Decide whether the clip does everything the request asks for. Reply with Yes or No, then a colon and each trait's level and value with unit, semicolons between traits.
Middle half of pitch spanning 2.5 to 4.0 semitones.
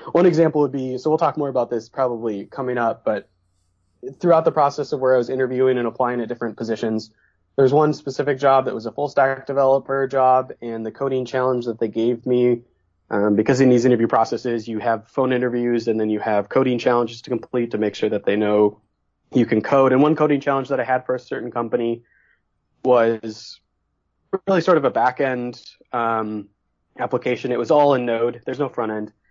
Yes: average, 3.2 semitones